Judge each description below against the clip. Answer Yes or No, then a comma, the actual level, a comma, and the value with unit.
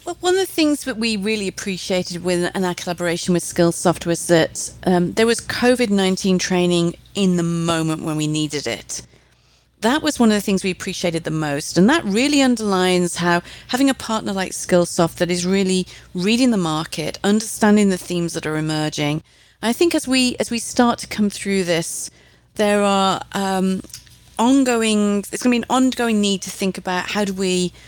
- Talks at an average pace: Yes, average, 195 wpm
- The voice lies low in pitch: No, high, 190 Hz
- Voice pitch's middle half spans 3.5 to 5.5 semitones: Yes, average, 4.2 semitones